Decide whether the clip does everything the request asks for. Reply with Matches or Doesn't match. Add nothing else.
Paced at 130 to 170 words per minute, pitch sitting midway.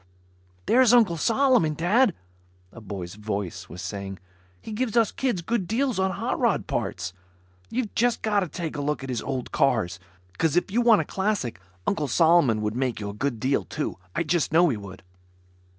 Doesn't match